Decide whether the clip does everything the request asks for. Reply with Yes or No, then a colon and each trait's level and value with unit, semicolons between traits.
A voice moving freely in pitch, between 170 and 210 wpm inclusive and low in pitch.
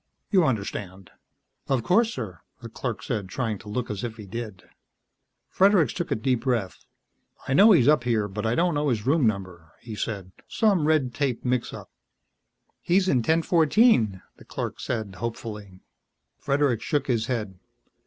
No: wide, 5.8 semitones; average, 160 wpm; low, 120 Hz